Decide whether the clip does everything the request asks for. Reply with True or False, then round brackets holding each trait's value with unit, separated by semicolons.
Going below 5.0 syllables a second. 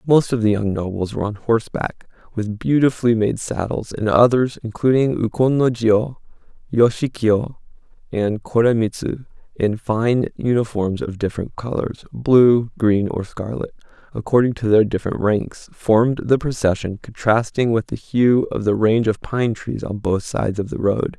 True (4.6 syllables/s)